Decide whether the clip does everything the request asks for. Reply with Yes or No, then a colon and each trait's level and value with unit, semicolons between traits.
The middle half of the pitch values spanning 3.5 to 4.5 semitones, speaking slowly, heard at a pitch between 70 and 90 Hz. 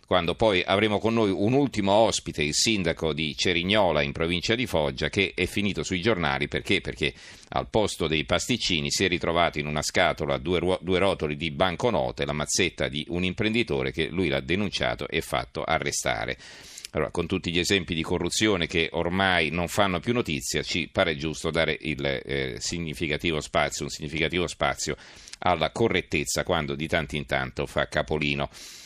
No: average, 3.8 semitones; fast, 170 wpm; very low, 85 Hz